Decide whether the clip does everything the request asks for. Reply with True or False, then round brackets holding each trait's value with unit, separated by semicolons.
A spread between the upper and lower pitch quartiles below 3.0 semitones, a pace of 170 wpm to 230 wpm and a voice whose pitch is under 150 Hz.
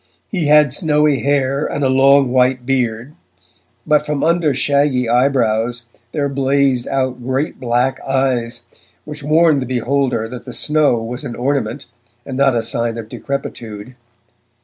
False (2.6 semitones; 150 wpm; 135 Hz)